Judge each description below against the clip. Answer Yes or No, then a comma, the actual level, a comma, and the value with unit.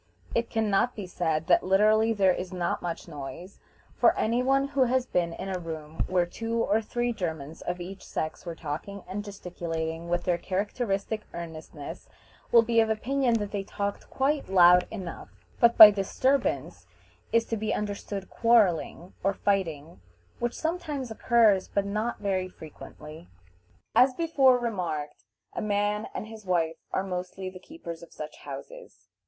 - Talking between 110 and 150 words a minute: No, average, 160 wpm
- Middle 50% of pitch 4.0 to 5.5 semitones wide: Yes, average, 4.7 semitones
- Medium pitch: No, high, 195 Hz